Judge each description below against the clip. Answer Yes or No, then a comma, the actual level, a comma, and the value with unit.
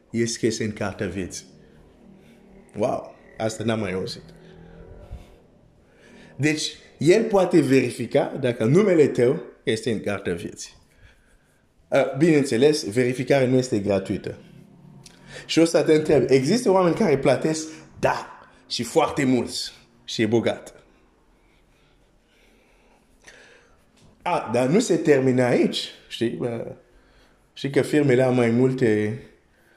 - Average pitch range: No, wide, 5.9 semitones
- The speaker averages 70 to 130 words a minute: Yes, average, 120 wpm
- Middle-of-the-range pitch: No, low, 125 Hz